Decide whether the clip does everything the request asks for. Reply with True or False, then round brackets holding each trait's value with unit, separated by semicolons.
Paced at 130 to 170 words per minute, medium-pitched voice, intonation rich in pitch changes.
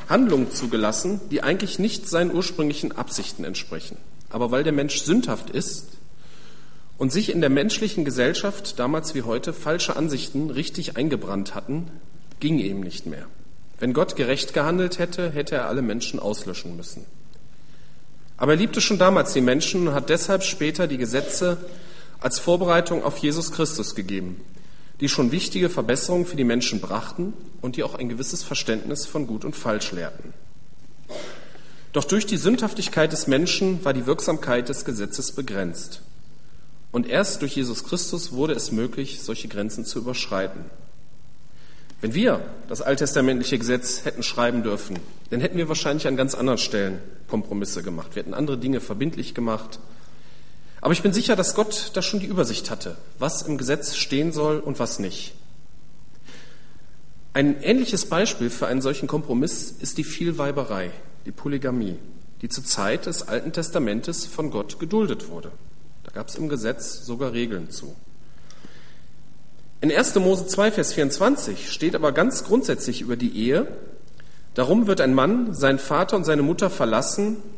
True (155 wpm; 145 Hz; 6.4 semitones)